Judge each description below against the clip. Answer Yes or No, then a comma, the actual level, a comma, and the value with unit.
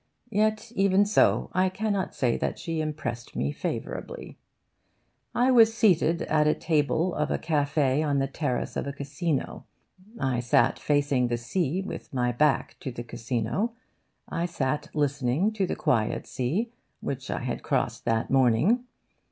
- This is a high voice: No, medium, 150 Hz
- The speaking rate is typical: Yes, average, 155 wpm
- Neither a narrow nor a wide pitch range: No, wide, 6.4 semitones